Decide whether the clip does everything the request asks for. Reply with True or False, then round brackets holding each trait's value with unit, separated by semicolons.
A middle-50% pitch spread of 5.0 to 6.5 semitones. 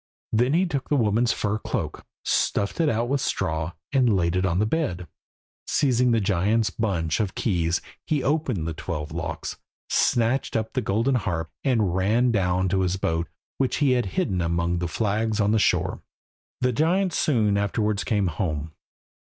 True (5.6 semitones)